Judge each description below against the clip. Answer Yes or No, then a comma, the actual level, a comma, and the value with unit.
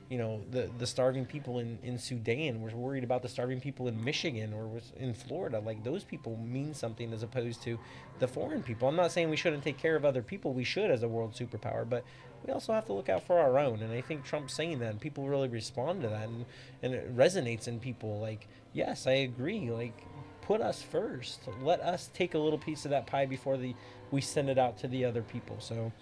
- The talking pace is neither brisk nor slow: No, fast, 240 wpm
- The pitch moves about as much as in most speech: Yes, average, 3.2 semitones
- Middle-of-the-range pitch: No, low, 125 Hz